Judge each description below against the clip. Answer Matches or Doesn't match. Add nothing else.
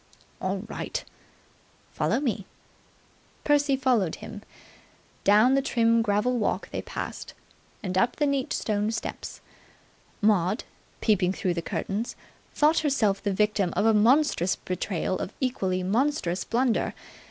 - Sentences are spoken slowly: Matches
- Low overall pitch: Doesn't match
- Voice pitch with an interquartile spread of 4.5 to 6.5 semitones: Matches